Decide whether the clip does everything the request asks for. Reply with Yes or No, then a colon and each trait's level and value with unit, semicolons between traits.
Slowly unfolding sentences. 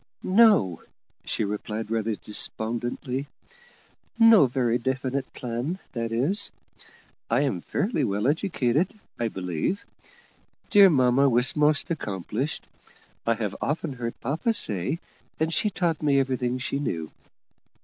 Yes: slow, 120 wpm